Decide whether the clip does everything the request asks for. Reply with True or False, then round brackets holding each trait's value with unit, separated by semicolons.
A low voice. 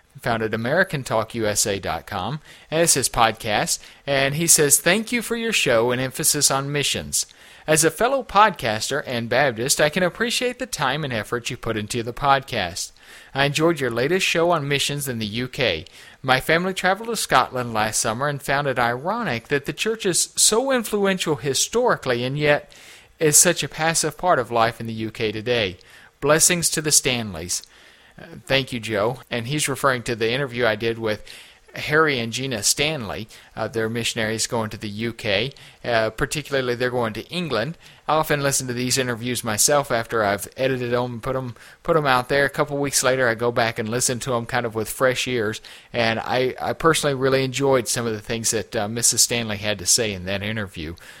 True (130 Hz)